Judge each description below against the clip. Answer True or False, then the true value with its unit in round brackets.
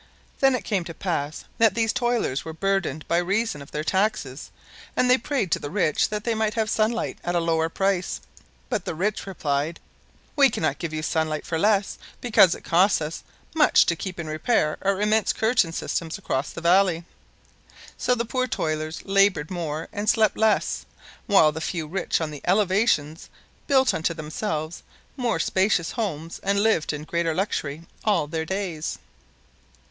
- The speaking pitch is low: False (180 Hz)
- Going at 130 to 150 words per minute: False (175 wpm)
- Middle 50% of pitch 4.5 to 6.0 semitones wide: True (5.2 semitones)